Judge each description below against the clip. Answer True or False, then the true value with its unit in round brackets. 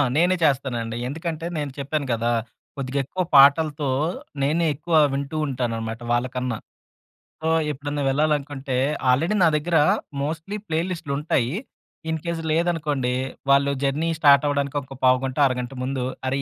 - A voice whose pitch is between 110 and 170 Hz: True (140 Hz)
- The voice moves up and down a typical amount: True (3.3 semitones)